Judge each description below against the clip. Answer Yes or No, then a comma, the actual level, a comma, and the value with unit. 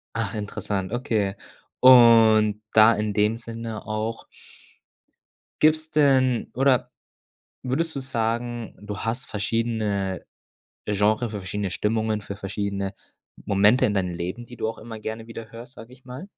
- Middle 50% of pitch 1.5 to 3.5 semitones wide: Yes, narrow, 2.6 semitones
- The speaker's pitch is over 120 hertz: No, low, 110 Hz